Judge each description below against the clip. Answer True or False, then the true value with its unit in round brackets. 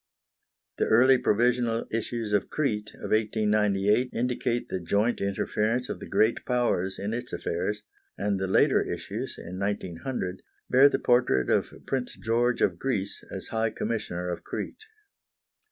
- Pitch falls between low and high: False (110 Hz)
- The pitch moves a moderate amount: True (3.6 semitones)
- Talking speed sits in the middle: True (145 wpm)